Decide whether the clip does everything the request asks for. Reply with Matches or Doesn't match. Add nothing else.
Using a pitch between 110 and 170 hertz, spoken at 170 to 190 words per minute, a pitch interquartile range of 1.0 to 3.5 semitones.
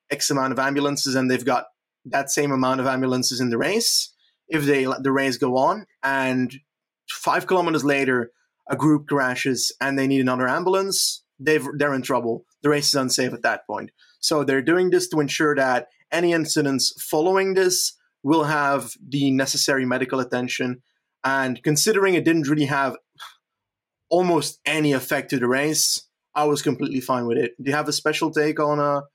Matches